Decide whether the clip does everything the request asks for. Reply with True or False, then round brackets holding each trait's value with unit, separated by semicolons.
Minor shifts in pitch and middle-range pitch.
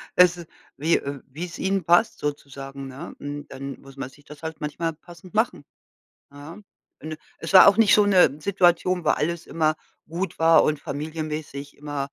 False (3.5 semitones; 155 Hz)